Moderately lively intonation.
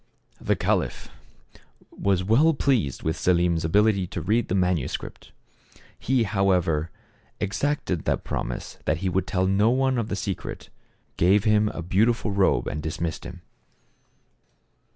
Yes: average, 4.0 semitones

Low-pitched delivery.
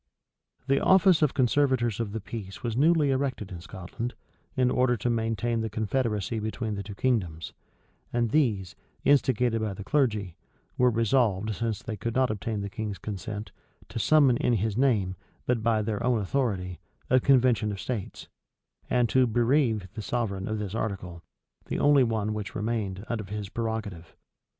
Yes: low, 110 Hz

